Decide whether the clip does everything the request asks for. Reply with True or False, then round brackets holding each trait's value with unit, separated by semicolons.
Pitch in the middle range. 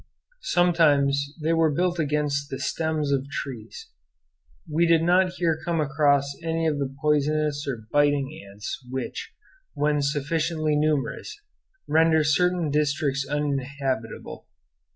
True (150 Hz)